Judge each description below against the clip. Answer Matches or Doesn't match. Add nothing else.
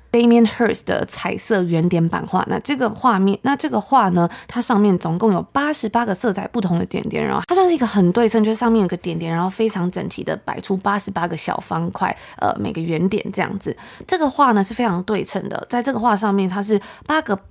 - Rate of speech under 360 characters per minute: Doesn't match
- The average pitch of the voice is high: Matches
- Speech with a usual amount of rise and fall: Matches